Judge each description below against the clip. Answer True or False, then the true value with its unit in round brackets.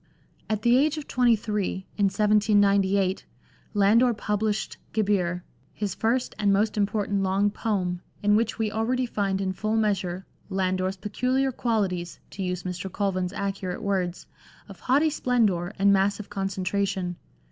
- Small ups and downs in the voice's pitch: True (2.3 semitones)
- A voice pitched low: False (200 Hz)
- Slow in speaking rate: False (145 wpm)